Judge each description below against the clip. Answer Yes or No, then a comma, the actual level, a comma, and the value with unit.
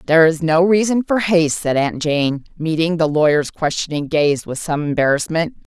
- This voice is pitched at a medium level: Yes, medium, 160 Hz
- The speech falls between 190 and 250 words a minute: No, average, 175 wpm